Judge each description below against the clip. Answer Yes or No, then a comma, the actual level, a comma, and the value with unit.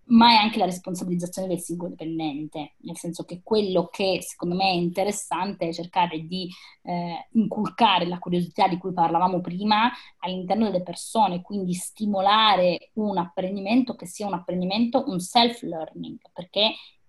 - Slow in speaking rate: No, average, 150 wpm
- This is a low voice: No, medium, 185 Hz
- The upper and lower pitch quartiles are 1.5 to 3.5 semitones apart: Yes, average, 3.2 semitones